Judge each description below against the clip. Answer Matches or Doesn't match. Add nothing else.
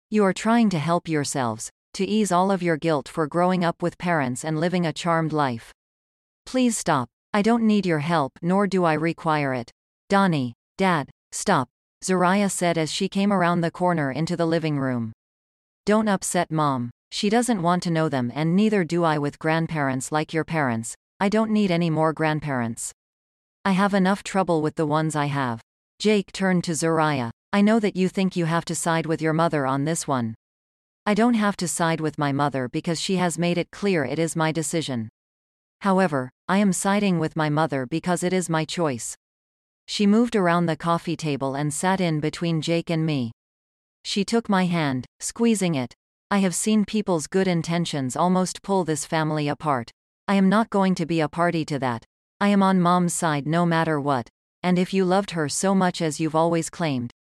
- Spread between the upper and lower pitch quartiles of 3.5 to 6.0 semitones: Matches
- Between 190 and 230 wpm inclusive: Matches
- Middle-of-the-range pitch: Matches